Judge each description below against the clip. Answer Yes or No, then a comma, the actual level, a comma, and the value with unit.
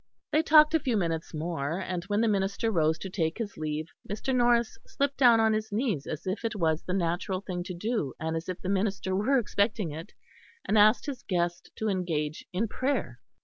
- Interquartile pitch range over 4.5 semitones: Yes, average, 5.0 semitones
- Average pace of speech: No, fast, 210 wpm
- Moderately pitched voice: No, high, 195 Hz